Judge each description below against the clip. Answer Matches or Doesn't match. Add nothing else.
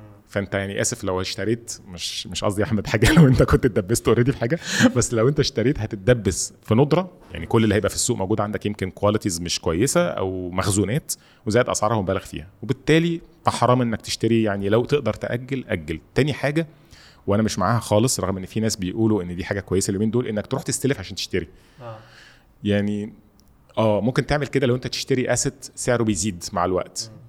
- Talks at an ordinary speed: Doesn't match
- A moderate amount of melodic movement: Matches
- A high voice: Doesn't match